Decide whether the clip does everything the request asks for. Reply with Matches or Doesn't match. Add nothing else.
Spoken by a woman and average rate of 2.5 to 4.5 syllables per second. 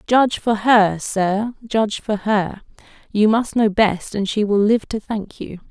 Matches